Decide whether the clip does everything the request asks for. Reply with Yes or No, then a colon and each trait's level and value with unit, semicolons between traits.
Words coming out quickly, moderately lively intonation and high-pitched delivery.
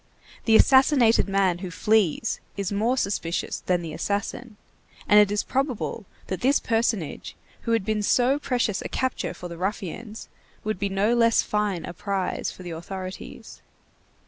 No: average, 160 wpm; average, 3.6 semitones; high, 210 Hz